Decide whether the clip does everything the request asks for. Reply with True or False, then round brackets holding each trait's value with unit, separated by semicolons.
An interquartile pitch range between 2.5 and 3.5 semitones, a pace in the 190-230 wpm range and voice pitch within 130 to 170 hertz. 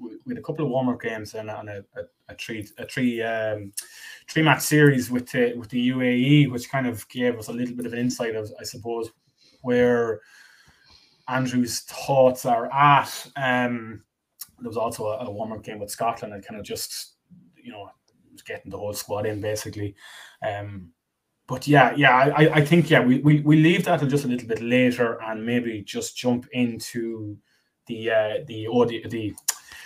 False (2.8 semitones; 195 wpm; 120 Hz)